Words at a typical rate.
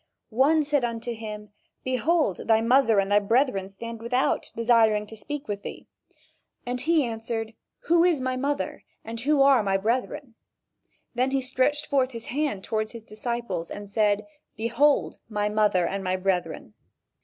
Yes: average, 160 wpm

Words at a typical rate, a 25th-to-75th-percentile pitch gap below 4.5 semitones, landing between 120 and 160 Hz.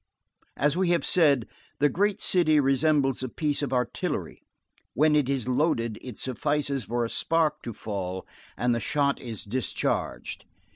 Yes: average, 155 wpm; average, 3.9 semitones; medium, 140 Hz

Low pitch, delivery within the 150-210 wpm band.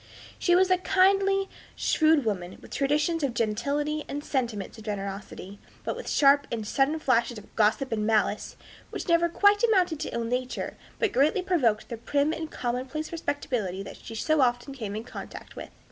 No: very high, 275 Hz; average, 175 wpm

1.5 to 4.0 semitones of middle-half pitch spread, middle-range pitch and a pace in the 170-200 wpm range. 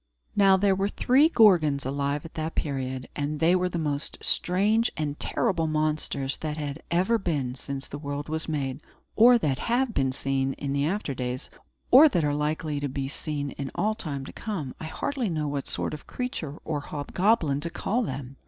No: average, 5.2 semitones; medium, 155 Hz; average, 190 wpm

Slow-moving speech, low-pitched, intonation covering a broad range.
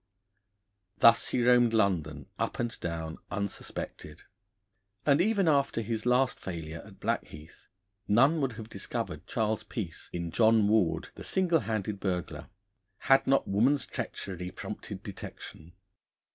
Yes: slow, 130 wpm; low, 110 Hz; wide, 5.9 semitones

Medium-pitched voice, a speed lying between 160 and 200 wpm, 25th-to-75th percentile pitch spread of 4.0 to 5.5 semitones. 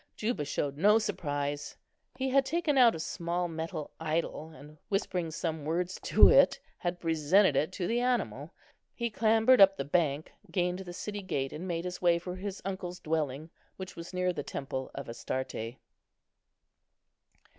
Yes: medium, 175 Hz; average, 165 wpm; average, 4.3 semitones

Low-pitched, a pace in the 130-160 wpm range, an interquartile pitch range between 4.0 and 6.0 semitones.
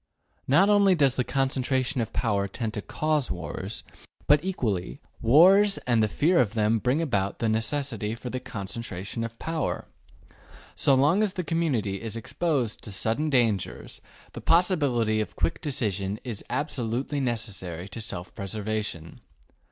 Yes: low, 120 Hz; average, 150 wpm; wide, 5.5 semitones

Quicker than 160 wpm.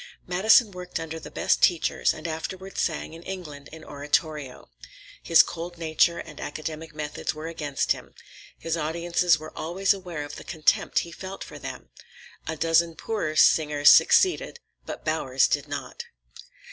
No: average, 155 wpm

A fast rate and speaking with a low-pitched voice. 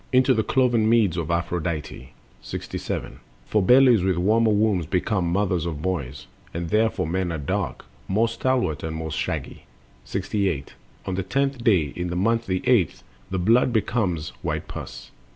No: average, 160 wpm; very low, 95 Hz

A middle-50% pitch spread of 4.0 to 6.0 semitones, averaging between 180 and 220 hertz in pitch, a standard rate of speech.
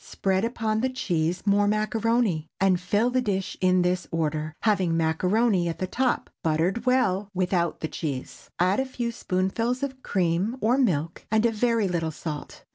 Yes: average, 5.1 semitones; high, 190 Hz; average, 170 wpm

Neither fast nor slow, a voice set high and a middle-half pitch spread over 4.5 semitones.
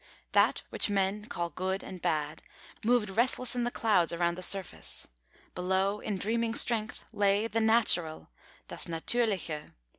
No: average, 145 wpm; high, 200 Hz; average, 4.2 semitones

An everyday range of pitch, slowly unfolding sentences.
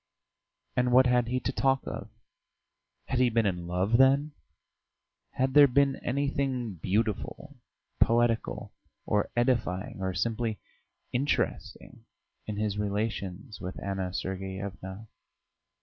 Yes: average, 4.8 semitones; slow, 115 wpm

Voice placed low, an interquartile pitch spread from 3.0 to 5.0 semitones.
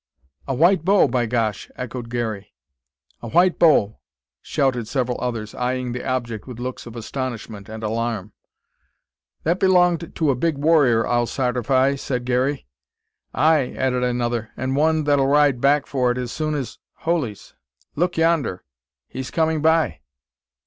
Yes: low, 130 Hz; average, 4.2 semitones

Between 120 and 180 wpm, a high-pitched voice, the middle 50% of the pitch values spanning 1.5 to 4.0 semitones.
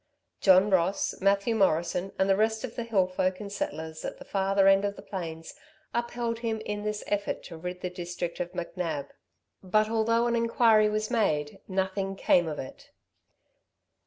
Yes: average, 175 wpm; high, 195 Hz; average, 3.3 semitones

